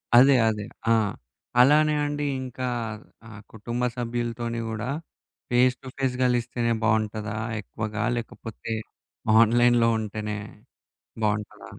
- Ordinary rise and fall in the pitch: No, narrow, 2.2 semitones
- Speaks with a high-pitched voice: No, low, 120 Hz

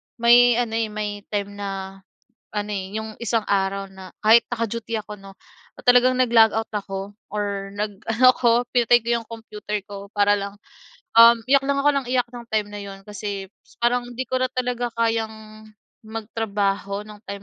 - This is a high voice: Yes, high, 215 Hz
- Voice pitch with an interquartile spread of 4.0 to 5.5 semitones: No, narrow, 2.6 semitones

